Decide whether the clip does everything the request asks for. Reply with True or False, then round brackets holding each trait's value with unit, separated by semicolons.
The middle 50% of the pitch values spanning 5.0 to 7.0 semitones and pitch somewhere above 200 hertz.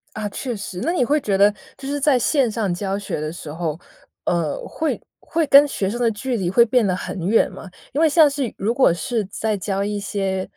True (5.5 semitones; 210 Hz)